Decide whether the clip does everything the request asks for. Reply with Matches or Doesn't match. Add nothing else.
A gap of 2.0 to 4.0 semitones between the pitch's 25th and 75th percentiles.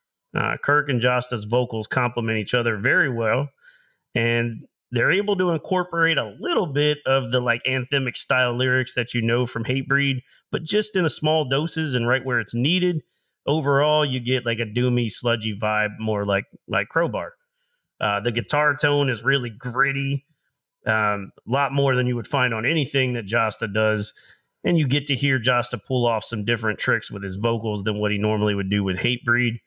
Matches